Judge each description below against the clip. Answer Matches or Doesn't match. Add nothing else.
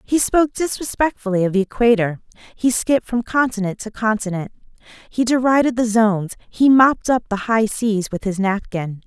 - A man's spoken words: Doesn't match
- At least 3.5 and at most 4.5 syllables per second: Doesn't match